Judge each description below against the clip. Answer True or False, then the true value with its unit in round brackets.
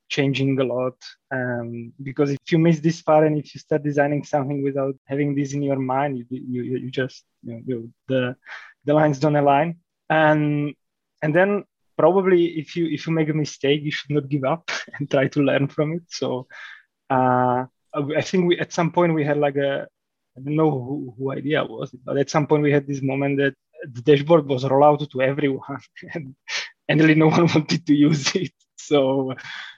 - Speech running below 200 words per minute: False (205 wpm)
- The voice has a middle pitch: True (145 Hz)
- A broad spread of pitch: False (2.4 semitones)